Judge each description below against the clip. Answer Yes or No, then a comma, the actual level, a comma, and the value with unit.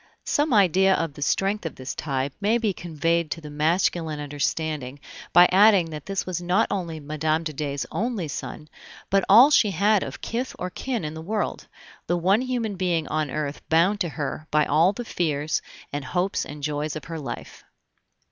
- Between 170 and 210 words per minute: Yes, average, 190 wpm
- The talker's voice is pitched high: No, medium, 165 Hz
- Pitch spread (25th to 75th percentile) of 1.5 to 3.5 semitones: No, average, 4.5 semitones